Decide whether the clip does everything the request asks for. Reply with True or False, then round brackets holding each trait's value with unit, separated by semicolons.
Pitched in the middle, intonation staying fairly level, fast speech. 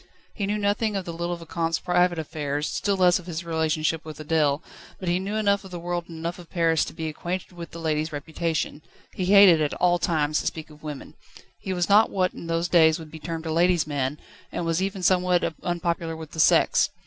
True (170 Hz; 2.2 semitones; 225 wpm)